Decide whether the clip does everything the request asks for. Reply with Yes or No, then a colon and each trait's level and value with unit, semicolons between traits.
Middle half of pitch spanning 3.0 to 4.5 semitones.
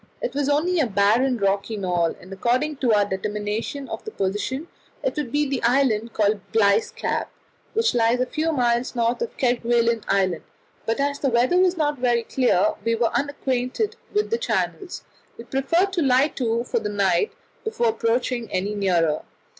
No: average, 5.3 semitones